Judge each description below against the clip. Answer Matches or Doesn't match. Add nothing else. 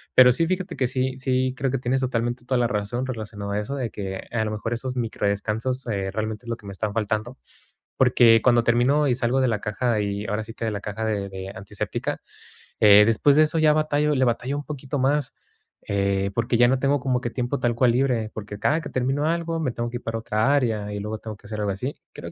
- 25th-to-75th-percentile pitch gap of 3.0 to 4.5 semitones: Matches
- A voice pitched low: Matches